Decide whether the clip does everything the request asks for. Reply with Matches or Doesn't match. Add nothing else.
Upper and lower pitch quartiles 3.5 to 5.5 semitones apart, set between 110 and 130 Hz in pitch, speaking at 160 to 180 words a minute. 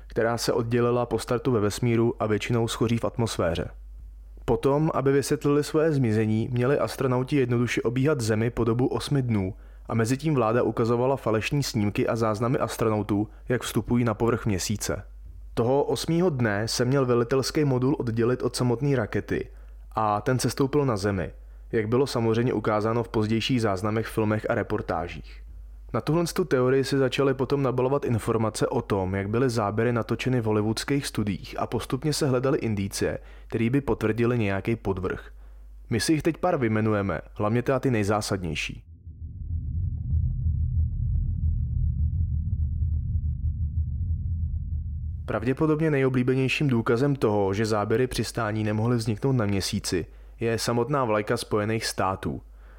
Doesn't match